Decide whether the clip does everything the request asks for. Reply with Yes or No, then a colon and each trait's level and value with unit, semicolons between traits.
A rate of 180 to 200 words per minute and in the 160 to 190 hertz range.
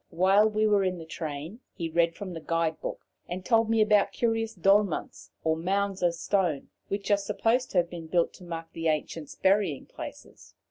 Yes: average, 195 wpm; medium, 185 Hz